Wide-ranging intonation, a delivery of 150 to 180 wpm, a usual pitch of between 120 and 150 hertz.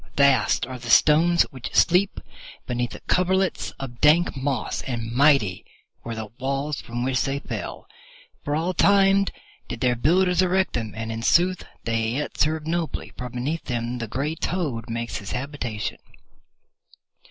Yes: wide, 5.8 semitones; average, 155 wpm; low, 135 Hz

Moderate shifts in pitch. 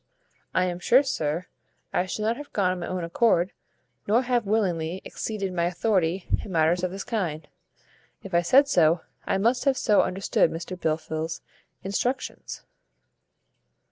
Yes: average, 4.2 semitones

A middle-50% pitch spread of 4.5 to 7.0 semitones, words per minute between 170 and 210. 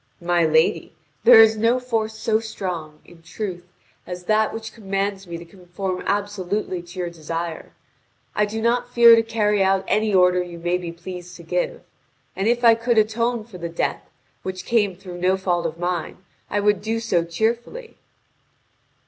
No: average, 4.0 semitones; average, 175 wpm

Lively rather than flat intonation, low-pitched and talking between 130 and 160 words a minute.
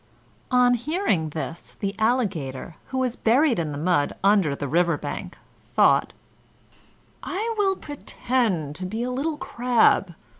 No: wide, 7.6 semitones; high, 220 Hz; average, 140 wpm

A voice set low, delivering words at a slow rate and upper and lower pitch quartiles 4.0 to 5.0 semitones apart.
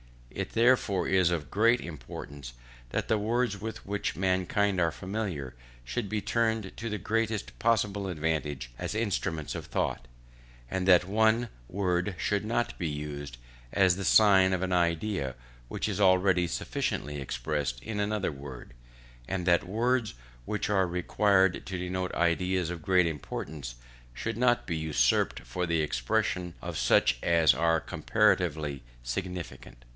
No: very low, 90 Hz; average, 145 wpm; average, 4.6 semitones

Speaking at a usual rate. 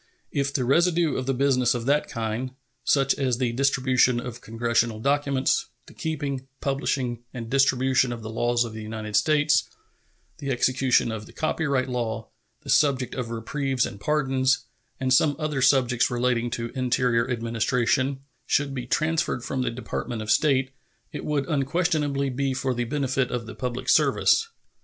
Yes: average, 160 wpm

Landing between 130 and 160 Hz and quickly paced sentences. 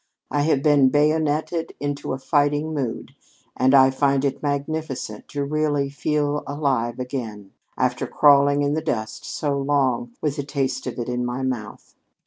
No: medium, 140 Hz; average, 160 wpm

